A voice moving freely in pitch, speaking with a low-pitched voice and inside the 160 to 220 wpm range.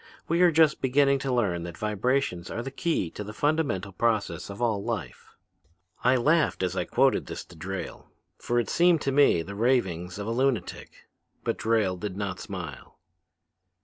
Yes: wide, 6.4 semitones; low, 115 Hz; average, 180 wpm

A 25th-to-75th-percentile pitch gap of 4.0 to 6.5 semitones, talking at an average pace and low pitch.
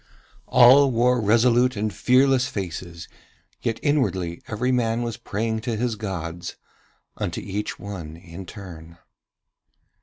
No: average, 5.2 semitones; slow, 120 wpm; low, 110 Hz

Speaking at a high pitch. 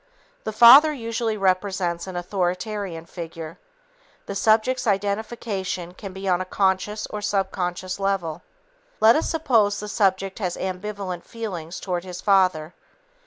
Yes: high, 195 Hz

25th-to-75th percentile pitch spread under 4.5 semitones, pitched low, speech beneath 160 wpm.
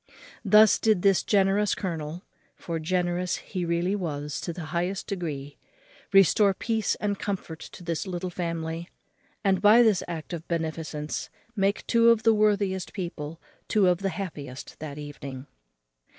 No: average, 3.6 semitones; medium, 180 Hz; average, 150 wpm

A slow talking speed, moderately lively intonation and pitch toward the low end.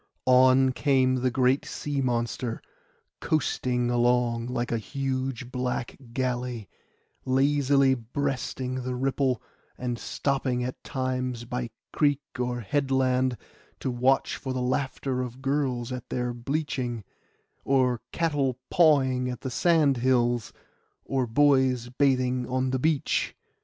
No: slow, 120 wpm; narrow, 1.6 semitones; low, 130 Hz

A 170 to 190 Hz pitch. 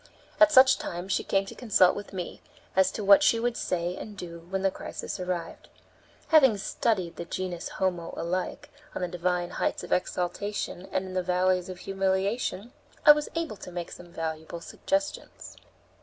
Yes: medium, 185 Hz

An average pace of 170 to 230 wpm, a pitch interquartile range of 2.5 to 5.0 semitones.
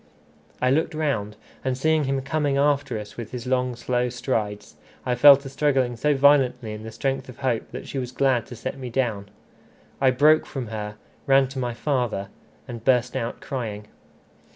Yes: average, 185 wpm; average, 2.8 semitones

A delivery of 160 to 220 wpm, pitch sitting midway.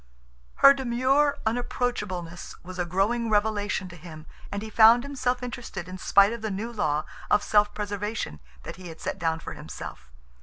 No: average, 165 wpm; high, 210 Hz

